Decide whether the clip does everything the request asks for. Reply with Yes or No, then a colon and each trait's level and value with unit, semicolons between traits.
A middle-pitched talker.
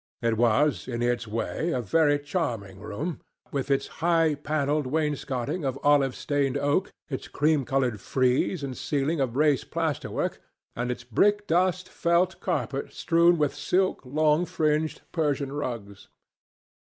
Yes: medium, 145 Hz